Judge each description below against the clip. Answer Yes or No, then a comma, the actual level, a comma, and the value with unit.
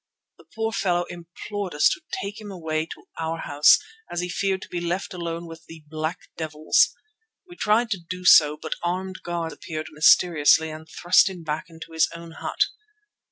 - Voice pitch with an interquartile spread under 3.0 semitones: Yes, narrow, 2.6 semitones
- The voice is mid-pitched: Yes, medium, 170 Hz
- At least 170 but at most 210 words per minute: Yes, average, 185 wpm